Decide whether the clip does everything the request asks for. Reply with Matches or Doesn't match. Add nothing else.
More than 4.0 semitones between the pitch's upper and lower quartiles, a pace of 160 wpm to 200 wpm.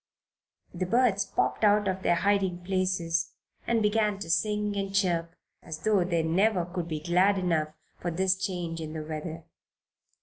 Doesn't match